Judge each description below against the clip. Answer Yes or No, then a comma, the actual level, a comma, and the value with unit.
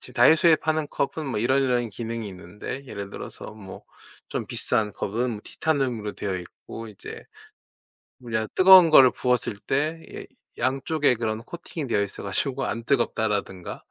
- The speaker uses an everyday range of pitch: Yes, average, 4.8 semitones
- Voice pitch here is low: Yes, low, 120 Hz